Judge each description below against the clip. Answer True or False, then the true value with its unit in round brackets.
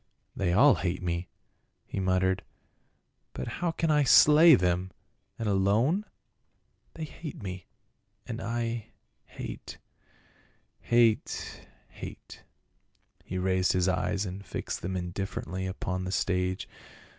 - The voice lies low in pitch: True (95 Hz)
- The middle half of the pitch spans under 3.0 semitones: False (4.3 semitones)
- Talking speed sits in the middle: False (125 wpm)